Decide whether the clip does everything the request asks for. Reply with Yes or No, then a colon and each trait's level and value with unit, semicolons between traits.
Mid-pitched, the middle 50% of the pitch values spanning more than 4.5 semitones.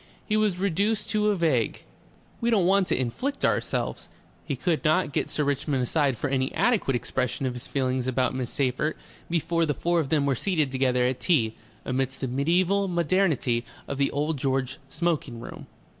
Yes: medium, 145 Hz; average, 5.3 semitones